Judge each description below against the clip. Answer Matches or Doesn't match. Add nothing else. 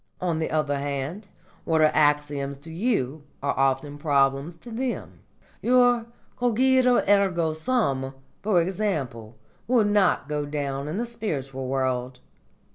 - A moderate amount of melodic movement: Doesn't match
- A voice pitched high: Doesn't match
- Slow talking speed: Matches